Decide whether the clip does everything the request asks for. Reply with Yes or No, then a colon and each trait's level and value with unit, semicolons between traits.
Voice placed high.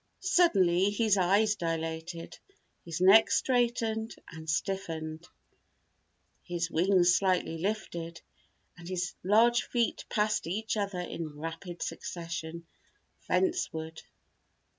No: medium, 180 Hz